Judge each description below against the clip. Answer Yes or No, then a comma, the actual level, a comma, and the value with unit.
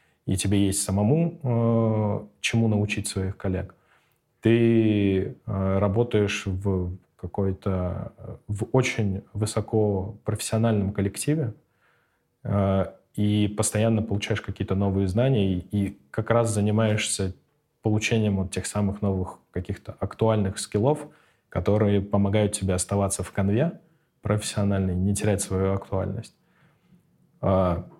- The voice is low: Yes, low, 105 Hz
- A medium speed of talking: No, slow, 105 wpm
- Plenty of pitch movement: No, narrow, 2.4 semitones